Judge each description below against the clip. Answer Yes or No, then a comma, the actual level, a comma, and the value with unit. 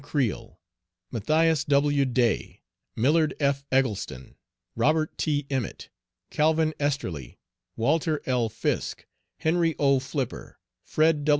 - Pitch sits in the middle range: Yes, medium, 145 Hz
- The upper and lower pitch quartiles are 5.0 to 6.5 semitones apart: No, average, 3.2 semitones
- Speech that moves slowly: Yes, slow, 100 wpm